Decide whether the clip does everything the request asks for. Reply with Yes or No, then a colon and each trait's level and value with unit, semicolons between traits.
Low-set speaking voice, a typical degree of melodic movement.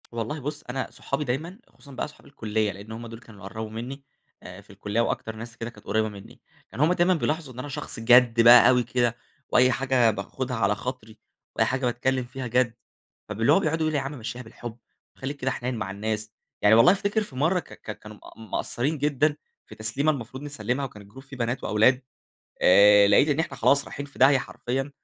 Yes: low, 125 Hz; average, 3.9 semitones